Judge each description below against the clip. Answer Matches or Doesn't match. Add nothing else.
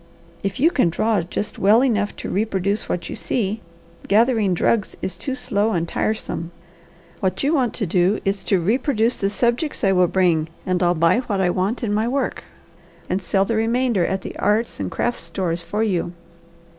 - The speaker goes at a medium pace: Matches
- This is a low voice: Doesn't match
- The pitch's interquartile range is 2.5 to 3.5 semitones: Doesn't match